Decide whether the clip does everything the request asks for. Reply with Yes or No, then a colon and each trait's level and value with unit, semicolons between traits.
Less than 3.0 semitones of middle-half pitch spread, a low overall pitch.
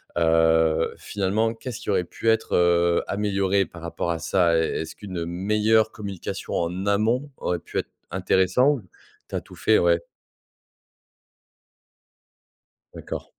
No: average, 3.9 semitones; very low, 95 Hz